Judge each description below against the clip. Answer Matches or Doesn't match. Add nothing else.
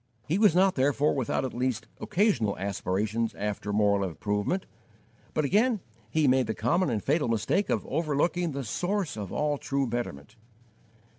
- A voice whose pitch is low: Matches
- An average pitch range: Doesn't match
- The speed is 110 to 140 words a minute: Doesn't match